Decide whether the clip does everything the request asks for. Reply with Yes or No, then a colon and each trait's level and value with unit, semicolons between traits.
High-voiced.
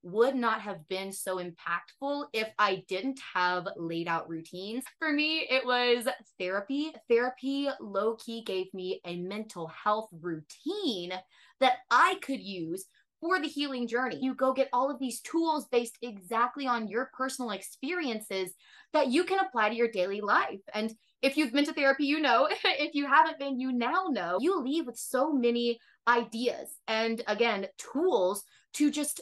Yes: high, 240 Hz